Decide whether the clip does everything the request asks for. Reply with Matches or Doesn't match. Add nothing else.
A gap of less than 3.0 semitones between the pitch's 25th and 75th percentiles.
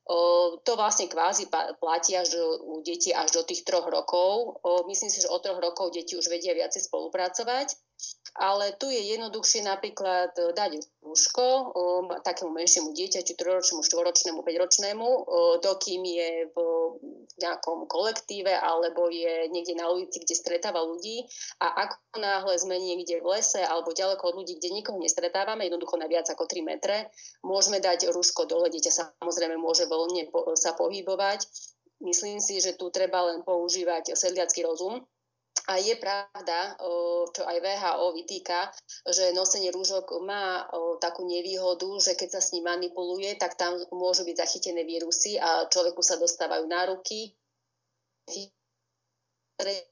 Matches